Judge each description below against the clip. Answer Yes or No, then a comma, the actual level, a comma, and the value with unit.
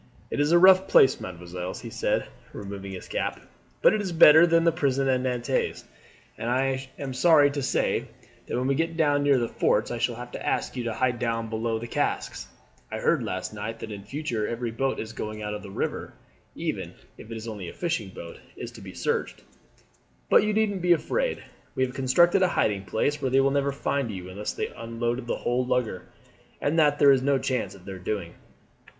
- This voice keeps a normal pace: No, fast, 215 wpm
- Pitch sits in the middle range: No, low, 125 Hz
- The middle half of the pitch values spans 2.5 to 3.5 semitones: No, average, 4.6 semitones